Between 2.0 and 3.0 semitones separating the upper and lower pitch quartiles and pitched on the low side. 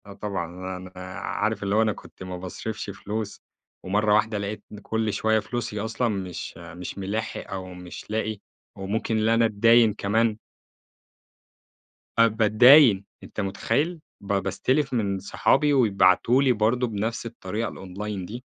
Yes: narrow, 2.5 semitones; low, 105 Hz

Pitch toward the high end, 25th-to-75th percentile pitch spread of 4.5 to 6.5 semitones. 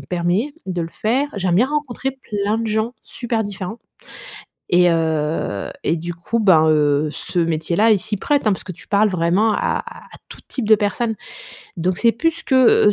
Yes: high, 200 Hz; average, 5.2 semitones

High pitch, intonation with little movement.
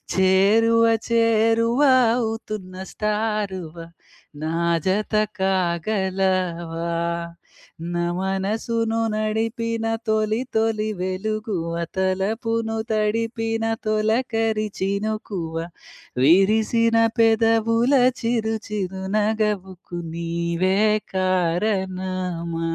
No: high, 210 Hz; average, 3.2 semitones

